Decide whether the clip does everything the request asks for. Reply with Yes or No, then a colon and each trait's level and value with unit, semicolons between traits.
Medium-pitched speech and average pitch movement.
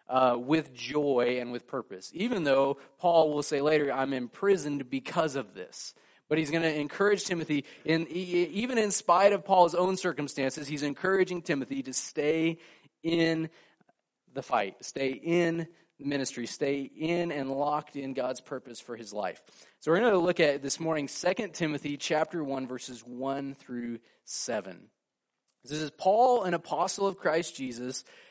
Yes: medium, 150 Hz; average, 4.2 semitones